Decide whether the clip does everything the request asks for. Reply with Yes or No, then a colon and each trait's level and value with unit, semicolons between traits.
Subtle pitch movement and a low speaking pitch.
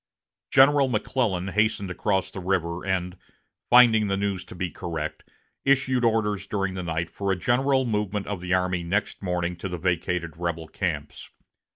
No: average, 3.5 semitones; very low, 95 Hz